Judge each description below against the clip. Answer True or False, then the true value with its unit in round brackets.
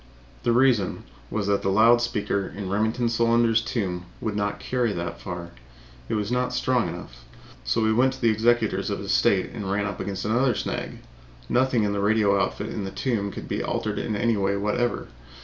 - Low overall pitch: True (105 Hz)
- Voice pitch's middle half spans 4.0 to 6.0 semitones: False (3.0 semitones)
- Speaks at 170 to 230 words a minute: True (200 wpm)